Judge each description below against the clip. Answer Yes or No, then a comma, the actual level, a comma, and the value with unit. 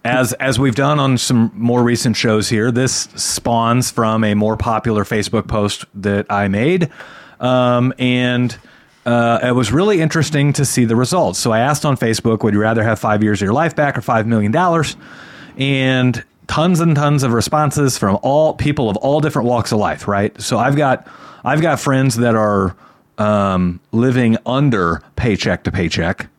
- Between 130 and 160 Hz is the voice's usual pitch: No, low, 120 Hz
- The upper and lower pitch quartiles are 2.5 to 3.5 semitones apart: No, average, 3.9 semitones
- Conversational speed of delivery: Yes, average, 180 wpm